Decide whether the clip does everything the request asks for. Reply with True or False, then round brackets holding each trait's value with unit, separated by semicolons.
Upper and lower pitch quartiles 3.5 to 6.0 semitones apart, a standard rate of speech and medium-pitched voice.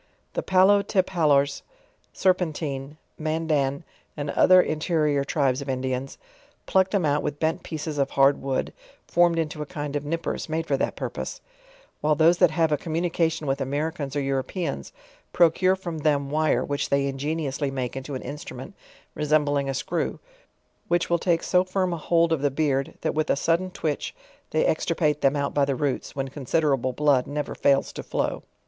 False (3.1 semitones; 175 wpm; 150 Hz)